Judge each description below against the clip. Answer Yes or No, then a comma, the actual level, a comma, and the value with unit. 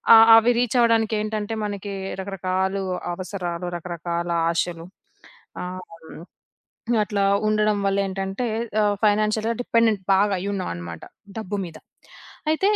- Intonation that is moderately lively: Yes, average, 3.0 semitones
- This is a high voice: Yes, high, 200 Hz